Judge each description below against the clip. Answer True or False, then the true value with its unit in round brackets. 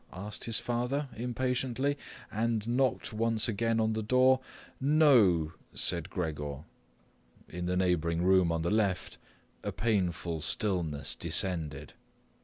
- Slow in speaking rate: True (120 wpm)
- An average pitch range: False (5.7 semitones)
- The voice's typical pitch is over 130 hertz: False (105 Hz)